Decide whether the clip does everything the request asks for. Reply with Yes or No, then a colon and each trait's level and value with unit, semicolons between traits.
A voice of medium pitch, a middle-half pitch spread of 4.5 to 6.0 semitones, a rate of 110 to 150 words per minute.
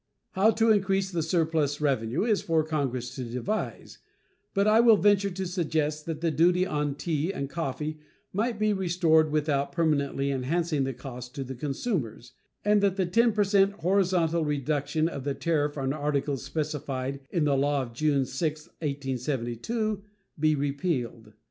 No: medium, 155 Hz; average, 4.9 semitones; average, 160 wpm